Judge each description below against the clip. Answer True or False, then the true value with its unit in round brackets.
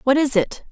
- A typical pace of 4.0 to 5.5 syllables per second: True (5.4 syllables/s)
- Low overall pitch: False (260 Hz)